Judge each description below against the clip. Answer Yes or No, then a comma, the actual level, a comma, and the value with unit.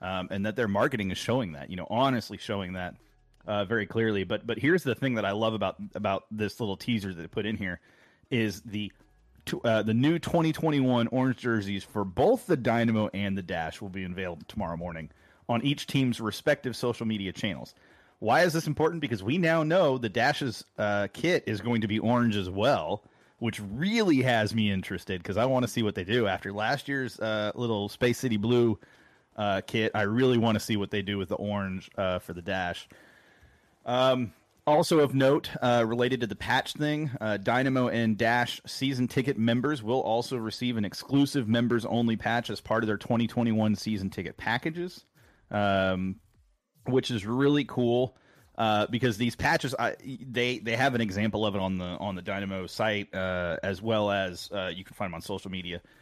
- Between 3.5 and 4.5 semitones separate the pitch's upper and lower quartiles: Yes, average, 3.8 semitones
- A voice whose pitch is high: No, low, 110 Hz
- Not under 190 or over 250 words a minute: Yes, average, 200 wpm